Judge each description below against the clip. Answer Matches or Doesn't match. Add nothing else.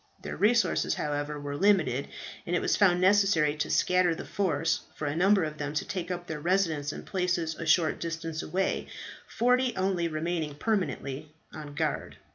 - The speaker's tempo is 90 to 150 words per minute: Doesn't match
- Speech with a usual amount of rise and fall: Matches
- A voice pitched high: Doesn't match